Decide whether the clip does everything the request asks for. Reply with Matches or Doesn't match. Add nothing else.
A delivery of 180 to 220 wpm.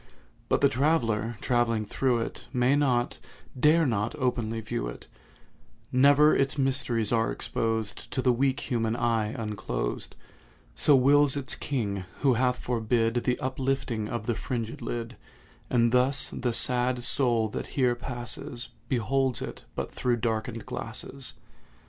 Doesn't match